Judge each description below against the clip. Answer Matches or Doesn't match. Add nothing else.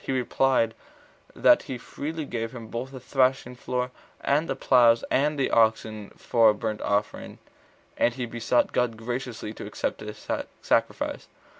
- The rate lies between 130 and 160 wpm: Matches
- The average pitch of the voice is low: Matches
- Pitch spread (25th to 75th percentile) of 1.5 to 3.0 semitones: Matches